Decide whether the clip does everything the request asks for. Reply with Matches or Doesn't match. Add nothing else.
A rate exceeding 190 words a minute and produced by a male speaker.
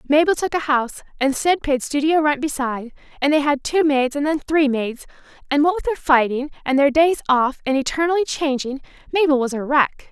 Doesn't match